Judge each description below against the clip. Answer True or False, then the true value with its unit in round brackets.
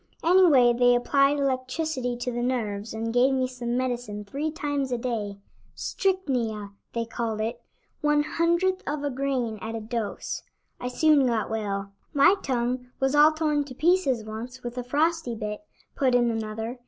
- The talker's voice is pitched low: False (250 Hz)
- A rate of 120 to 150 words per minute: False (165 wpm)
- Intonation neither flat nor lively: True (4.1 semitones)